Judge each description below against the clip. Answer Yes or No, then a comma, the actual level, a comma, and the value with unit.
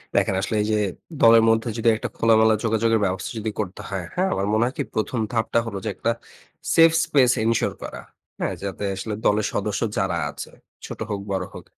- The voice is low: Yes, low, 110 Hz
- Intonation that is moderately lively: No, narrow, 2.3 semitones